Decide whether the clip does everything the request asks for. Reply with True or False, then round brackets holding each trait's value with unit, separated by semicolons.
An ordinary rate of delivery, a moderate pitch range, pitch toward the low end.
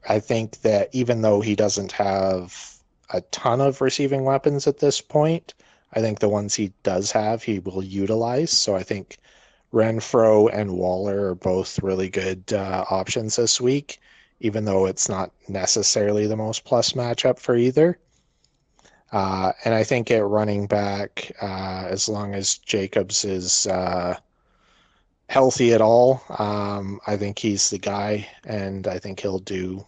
True (160 wpm; 3.6 semitones; 105 Hz)